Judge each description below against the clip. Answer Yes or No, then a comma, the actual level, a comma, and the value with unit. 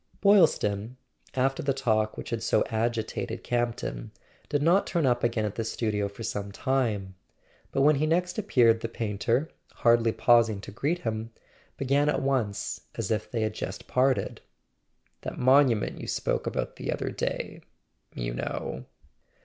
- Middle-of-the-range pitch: No, low, 120 Hz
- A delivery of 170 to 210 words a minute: No, average, 160 wpm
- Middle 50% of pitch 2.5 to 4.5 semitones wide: Yes, average, 4.0 semitones